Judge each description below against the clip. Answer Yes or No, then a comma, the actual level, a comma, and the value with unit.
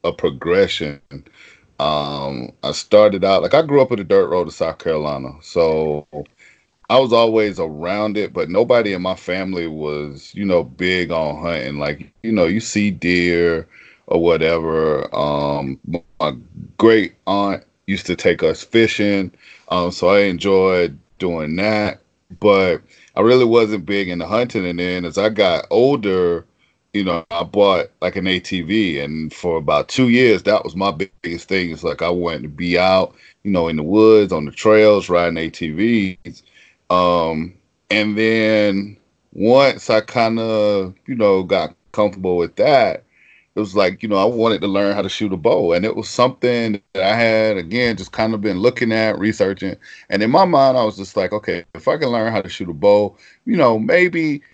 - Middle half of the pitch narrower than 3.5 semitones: No, average, 4.2 semitones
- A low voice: Yes, low, 100 Hz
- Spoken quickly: No, average, 185 wpm